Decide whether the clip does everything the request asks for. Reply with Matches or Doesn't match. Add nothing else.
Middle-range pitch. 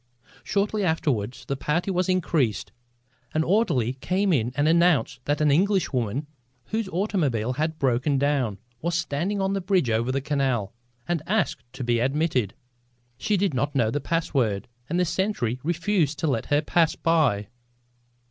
Matches